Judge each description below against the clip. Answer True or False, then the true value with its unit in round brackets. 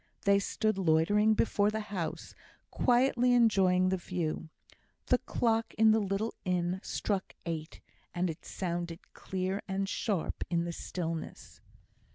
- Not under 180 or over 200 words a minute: False (135 wpm)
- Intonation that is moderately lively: True (3.7 semitones)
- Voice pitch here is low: False (190 Hz)